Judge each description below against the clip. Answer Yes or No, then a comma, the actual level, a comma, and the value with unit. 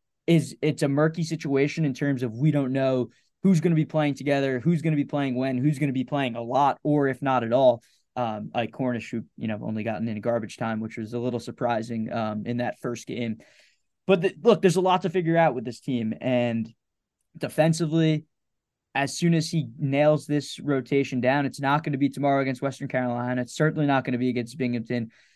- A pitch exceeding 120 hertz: Yes, low, 135 Hz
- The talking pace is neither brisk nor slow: No, fast, 225 wpm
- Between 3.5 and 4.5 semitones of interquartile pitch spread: Yes, average, 3.9 semitones